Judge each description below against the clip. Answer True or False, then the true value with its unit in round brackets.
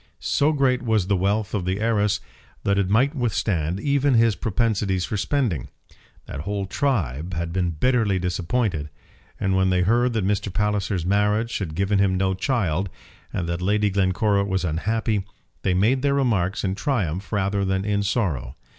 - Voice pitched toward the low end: True (100 Hz)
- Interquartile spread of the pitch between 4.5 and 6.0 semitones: False (3.3 semitones)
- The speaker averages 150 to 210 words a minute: True (170 wpm)